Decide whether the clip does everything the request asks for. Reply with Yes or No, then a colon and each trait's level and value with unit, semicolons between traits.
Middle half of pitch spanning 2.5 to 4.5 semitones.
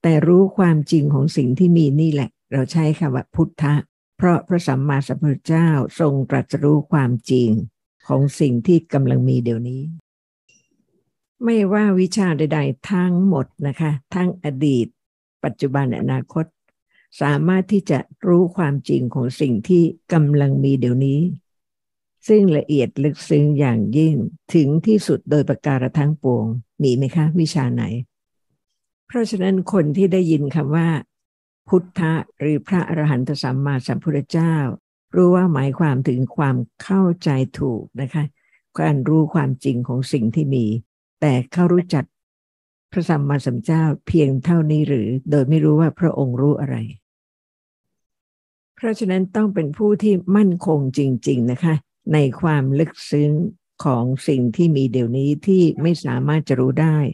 Yes: average, 4.0 semitones